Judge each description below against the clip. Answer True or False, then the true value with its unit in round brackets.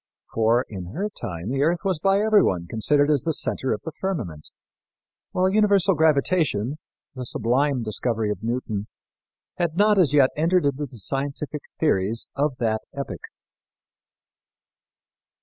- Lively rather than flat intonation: True (6.8 semitones)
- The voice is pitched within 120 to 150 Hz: True (140 Hz)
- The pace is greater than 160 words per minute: False (140 wpm)